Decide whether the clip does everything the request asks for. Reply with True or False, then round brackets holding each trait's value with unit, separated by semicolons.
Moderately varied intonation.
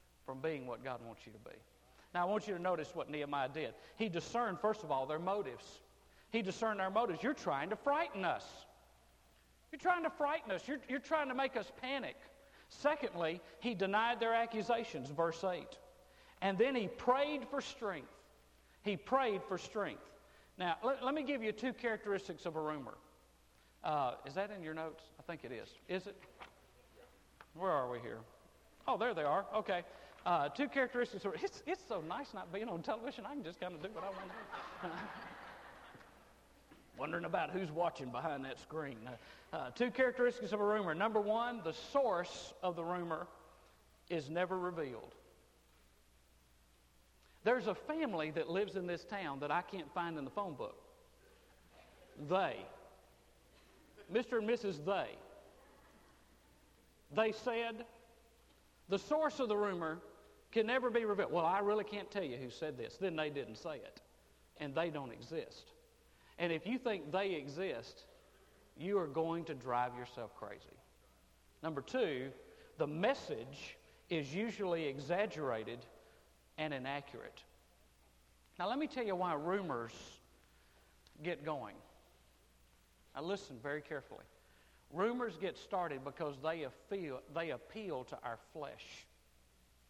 False (8.8 semitones)